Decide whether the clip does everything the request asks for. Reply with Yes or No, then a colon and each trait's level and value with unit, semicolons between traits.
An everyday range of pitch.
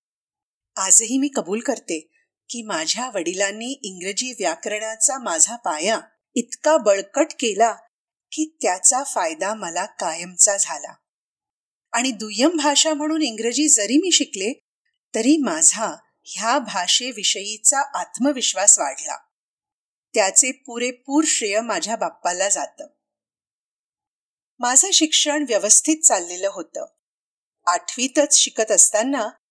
No: wide, 6.1 semitones